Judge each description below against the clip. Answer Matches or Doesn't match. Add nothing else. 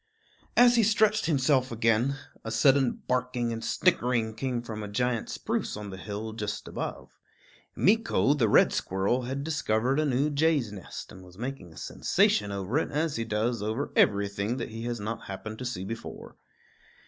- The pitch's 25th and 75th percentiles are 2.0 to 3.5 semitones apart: Doesn't match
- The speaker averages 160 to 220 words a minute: Matches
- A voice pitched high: Doesn't match